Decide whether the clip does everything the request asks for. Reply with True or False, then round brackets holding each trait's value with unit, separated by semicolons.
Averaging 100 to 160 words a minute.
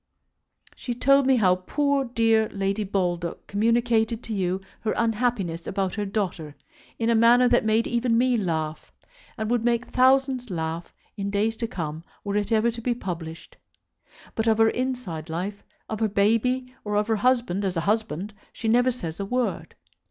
False (175 wpm)